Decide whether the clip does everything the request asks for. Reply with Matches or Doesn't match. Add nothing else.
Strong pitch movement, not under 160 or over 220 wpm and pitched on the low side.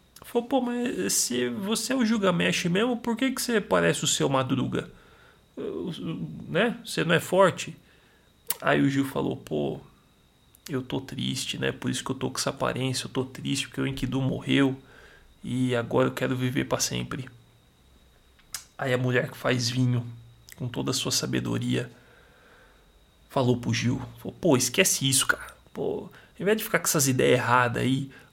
Matches